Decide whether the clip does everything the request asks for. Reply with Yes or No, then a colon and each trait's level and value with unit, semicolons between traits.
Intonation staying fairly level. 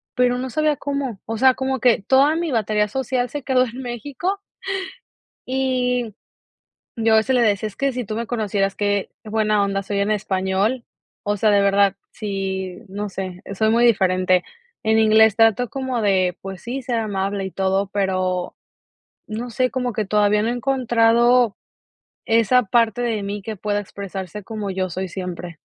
No: average, 4.0 semitones